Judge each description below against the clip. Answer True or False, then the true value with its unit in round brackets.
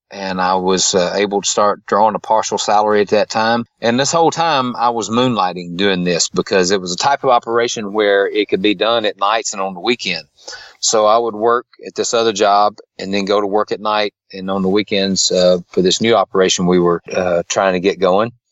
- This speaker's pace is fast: True (235 wpm)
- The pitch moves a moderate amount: True (3.5 semitones)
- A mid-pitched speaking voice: False (105 Hz)